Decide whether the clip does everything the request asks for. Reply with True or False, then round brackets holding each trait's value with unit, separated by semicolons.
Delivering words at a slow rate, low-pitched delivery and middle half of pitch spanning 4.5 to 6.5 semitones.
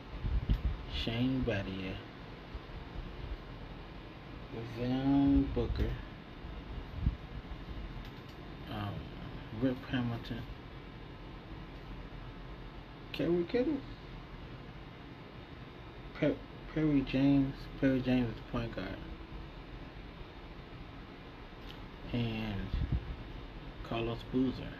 True (50 wpm; 125 Hz; 5.6 semitones)